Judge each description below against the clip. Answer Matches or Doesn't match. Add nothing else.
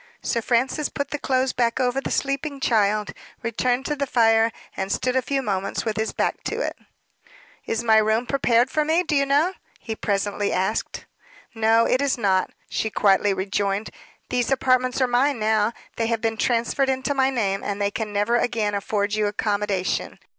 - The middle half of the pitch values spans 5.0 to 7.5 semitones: Doesn't match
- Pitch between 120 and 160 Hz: Doesn't match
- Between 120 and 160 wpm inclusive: Doesn't match